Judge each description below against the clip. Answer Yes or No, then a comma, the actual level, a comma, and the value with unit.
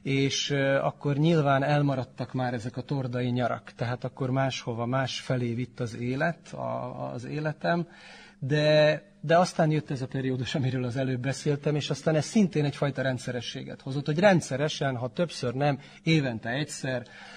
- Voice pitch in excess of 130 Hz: Yes, medium, 140 Hz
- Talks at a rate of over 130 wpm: Yes, fast, 155 wpm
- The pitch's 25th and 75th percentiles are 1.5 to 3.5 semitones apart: Yes, average, 3.1 semitones